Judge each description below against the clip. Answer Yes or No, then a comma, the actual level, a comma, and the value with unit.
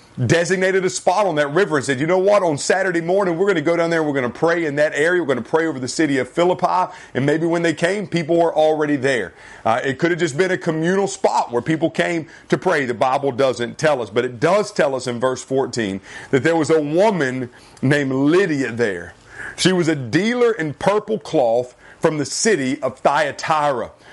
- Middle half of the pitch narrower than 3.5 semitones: No, average, 4.7 semitones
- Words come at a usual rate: No, fast, 230 wpm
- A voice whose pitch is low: No, medium, 160 Hz